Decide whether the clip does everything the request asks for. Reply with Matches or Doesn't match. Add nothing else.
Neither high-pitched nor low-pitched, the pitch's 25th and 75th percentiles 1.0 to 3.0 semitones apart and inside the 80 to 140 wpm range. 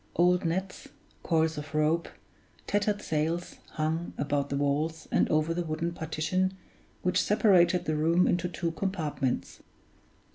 Matches